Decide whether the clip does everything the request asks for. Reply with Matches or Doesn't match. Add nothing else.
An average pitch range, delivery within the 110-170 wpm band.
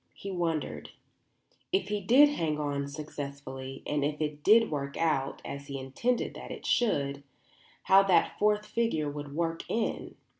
Doesn't match